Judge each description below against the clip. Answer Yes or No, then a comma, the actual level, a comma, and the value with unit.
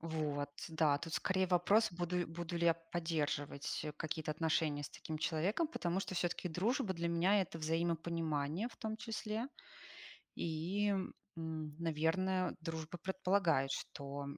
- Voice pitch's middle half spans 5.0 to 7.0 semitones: No, average, 3.0 semitones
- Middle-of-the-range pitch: Yes, medium, 170 Hz